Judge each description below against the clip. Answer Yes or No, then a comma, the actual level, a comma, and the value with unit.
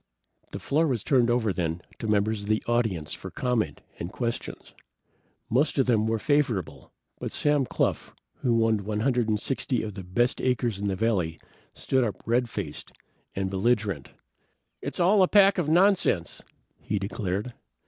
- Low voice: Yes, low, 115 Hz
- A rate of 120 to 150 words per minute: No, average, 170 wpm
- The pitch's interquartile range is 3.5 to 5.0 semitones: Yes, average, 4.2 semitones